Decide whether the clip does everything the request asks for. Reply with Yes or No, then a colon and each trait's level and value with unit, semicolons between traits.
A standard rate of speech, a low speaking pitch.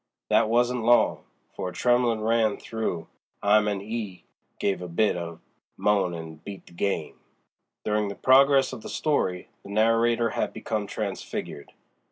Yes: average, 160 wpm; low, 105 Hz